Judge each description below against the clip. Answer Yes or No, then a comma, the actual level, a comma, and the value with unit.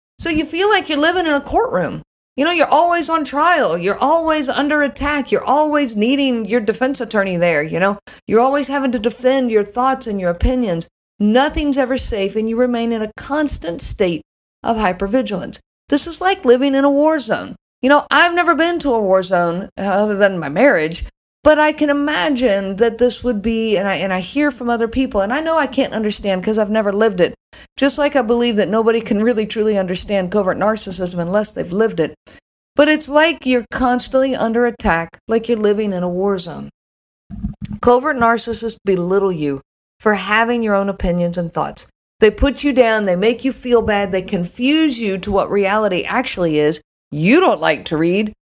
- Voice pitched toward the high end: Yes, high, 230 Hz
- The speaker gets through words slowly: No, average, 200 wpm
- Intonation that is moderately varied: No, wide, 5.9 semitones